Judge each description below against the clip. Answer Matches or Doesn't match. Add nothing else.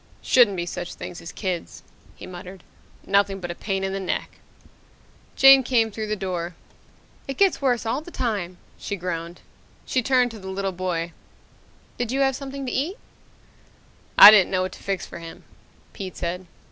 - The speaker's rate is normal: Matches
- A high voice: Matches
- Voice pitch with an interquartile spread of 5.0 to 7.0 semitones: Matches